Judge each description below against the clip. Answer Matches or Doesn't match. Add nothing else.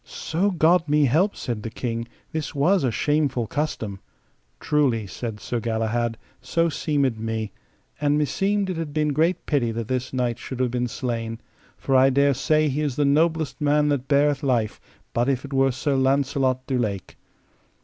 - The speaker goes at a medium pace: Matches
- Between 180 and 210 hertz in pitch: Doesn't match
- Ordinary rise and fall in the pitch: Matches